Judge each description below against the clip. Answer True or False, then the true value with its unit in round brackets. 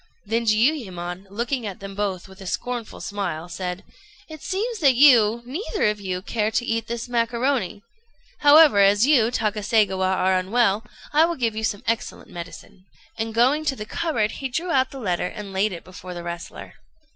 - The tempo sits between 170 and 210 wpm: True (180 wpm)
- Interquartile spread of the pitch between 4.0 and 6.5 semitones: True (4.7 semitones)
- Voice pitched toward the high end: True (220 Hz)